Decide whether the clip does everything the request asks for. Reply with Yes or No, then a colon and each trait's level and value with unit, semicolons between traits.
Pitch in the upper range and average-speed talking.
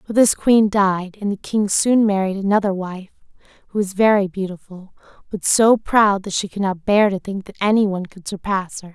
No: high, 200 Hz; fast, 210 wpm